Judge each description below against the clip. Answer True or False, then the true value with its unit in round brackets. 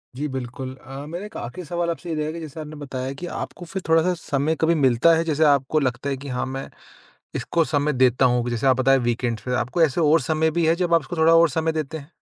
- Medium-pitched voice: True (150 Hz)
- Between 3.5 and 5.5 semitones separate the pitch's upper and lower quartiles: True (3.8 semitones)